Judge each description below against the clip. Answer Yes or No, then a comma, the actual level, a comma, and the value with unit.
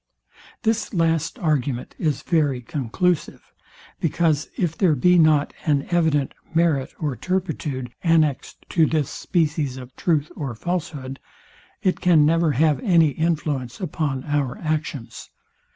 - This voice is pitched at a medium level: Yes, medium, 155 Hz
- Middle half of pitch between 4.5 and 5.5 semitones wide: No, average, 3.2 semitones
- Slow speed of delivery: Yes, slow, 125 wpm